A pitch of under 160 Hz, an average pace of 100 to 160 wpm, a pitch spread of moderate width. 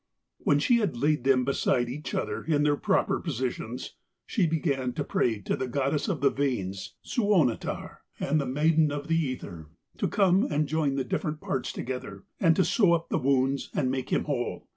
No: medium, 140 Hz; average, 190 wpm; average, 3.9 semitones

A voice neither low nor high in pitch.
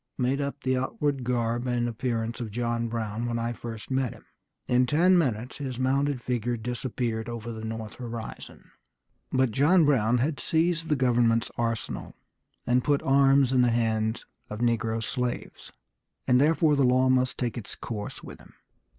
No: low, 125 Hz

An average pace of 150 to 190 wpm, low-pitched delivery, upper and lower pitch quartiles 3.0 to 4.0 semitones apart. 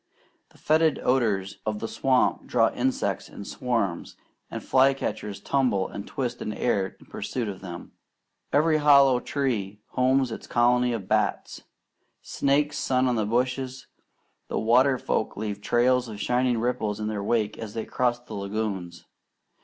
Yes: average, 155 wpm; low, 120 Hz; average, 3.7 semitones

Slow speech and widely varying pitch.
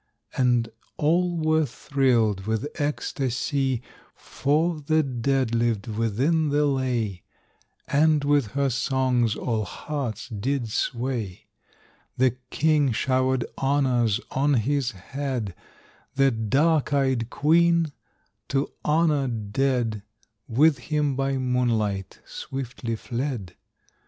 No: slow, 100 wpm; average, 3.8 semitones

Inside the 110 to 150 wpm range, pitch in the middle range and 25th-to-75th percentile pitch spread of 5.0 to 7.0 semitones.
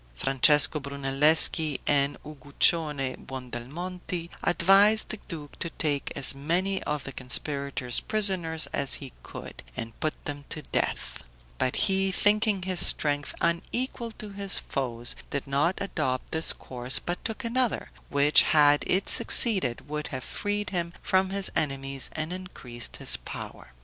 Yes: average, 140 wpm; medium, 155 Hz; wide, 5.4 semitones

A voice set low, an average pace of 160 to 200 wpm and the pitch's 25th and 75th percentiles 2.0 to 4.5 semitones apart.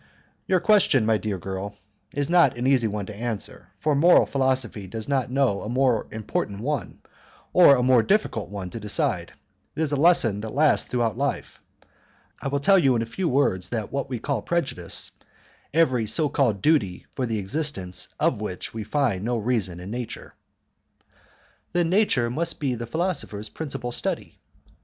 No: low, 125 Hz; average, 175 wpm; average, 5.1 semitones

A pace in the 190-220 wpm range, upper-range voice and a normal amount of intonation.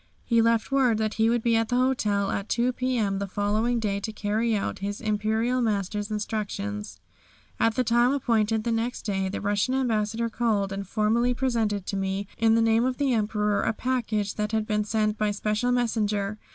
No: average, 195 wpm; high, 220 Hz; narrow, 2.2 semitones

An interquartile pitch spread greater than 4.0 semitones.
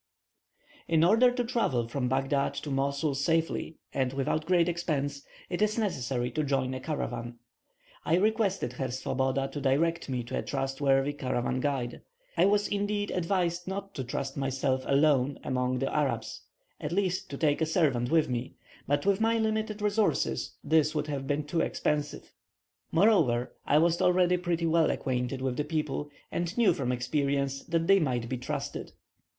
Yes: average, 4.7 semitones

